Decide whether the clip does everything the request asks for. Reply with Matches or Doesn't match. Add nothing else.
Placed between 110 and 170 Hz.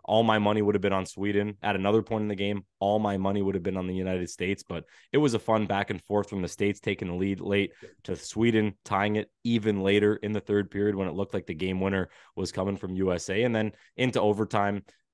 Doesn't match